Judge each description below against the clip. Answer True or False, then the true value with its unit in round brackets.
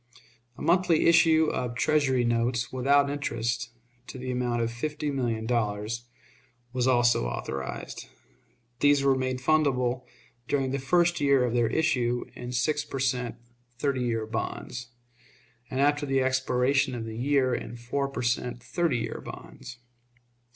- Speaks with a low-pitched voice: True (130 Hz)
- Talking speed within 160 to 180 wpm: False (145 wpm)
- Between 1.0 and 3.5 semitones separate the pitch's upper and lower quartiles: True (2.8 semitones)